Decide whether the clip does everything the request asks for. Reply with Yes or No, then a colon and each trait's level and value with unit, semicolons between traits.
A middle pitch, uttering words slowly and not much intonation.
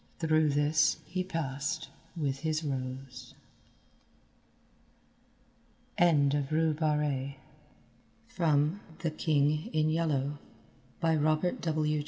Yes: medium, 150 Hz; slow, 90 wpm; narrow, 2.1 semitones